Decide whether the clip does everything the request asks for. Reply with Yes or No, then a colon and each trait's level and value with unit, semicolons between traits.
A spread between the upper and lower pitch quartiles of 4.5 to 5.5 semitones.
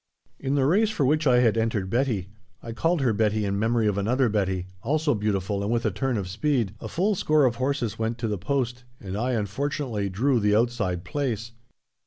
Yes: average, 4.8 semitones